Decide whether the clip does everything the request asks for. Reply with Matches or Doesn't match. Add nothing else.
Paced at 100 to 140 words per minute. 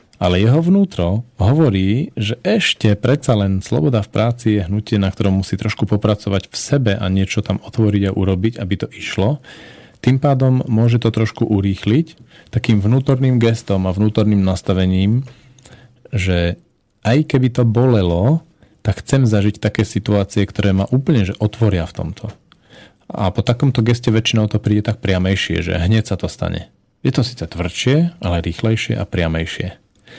Doesn't match